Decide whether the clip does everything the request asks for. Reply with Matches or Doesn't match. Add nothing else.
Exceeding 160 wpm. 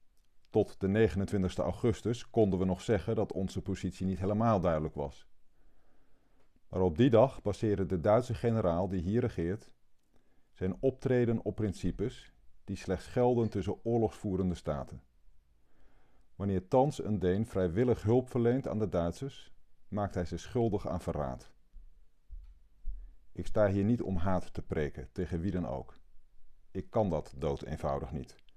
Doesn't match